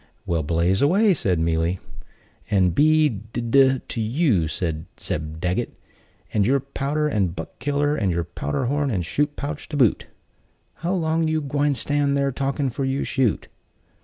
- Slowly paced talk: No, average, 165 wpm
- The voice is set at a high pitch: No, low, 135 Hz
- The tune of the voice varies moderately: No, wide, 8.0 semitones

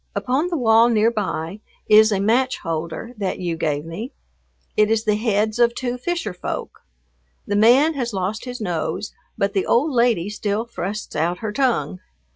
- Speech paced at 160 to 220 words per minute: Yes, average, 175 wpm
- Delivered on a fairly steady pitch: No, average, 3.8 semitones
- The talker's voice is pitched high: Yes, high, 215 Hz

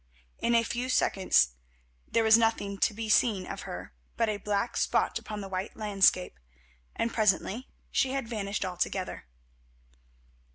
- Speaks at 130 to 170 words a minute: Yes, average, 150 wpm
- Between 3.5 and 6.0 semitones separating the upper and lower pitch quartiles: No, average, 3.0 semitones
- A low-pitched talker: No, high, 210 Hz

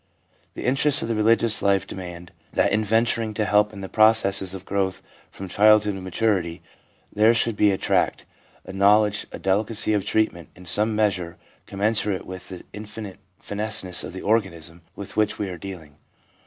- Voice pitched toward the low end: Yes, low, 105 Hz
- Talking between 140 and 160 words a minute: No, average, 180 wpm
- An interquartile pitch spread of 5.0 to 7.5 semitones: No, narrow, 2.4 semitones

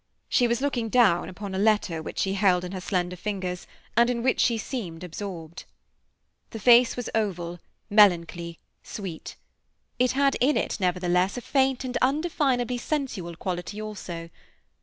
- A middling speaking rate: Yes, average, 155 wpm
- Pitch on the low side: No, high, 205 Hz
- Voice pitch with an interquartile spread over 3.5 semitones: Yes, wide, 5.5 semitones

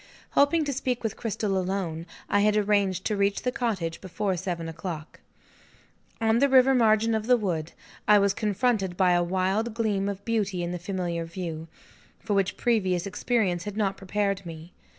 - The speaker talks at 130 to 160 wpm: No, average, 175 wpm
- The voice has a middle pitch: No, high, 200 Hz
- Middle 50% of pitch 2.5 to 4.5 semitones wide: Yes, average, 3.6 semitones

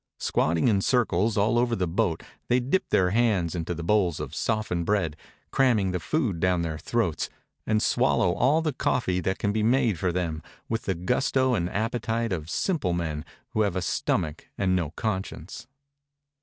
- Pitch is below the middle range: Yes, very low, 95 Hz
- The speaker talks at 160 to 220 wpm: Yes, average, 180 wpm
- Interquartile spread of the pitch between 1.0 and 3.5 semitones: No, average, 5.1 semitones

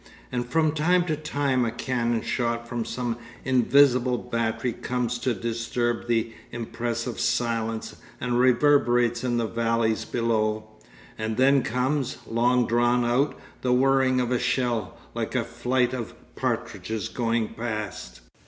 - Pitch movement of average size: No, narrow, 1.6 semitones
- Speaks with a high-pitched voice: No, low, 120 Hz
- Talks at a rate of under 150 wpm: Yes, slow, 135 wpm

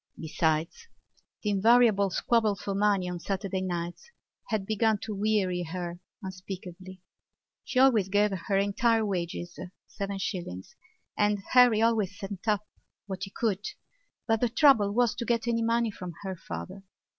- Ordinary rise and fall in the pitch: Yes, average, 3.3 semitones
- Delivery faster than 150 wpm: No, average, 140 wpm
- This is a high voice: Yes, high, 200 Hz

